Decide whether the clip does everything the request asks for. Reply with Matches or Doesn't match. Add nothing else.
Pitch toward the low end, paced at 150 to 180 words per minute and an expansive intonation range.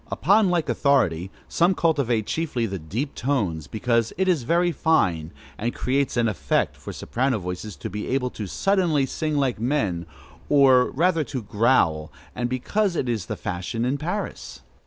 Matches